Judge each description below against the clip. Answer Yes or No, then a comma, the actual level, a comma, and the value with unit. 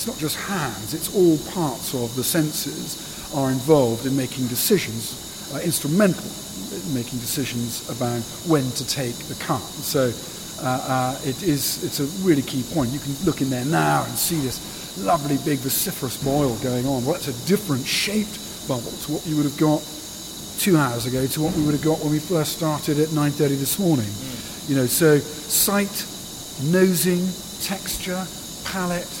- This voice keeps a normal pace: Yes, average, 180 wpm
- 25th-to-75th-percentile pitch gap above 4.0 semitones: Yes, average, 4.7 semitones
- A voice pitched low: No, medium, 150 Hz